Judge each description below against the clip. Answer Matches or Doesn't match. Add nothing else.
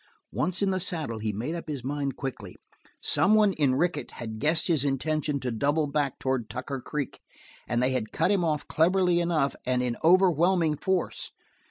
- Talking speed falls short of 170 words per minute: Doesn't match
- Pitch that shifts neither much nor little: Matches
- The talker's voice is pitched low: Doesn't match